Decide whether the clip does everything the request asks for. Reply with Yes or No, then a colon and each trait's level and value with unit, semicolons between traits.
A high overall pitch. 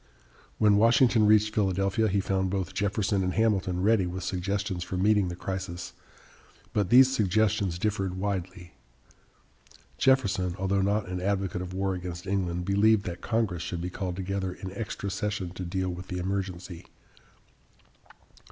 No: very low, 95 Hz